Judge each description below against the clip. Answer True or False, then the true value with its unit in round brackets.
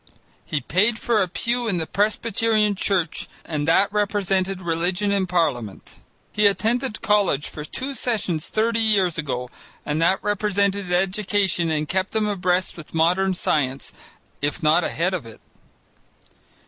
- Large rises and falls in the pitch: False (4.1 semitones)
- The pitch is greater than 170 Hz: True (190 Hz)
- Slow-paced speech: False (145 wpm)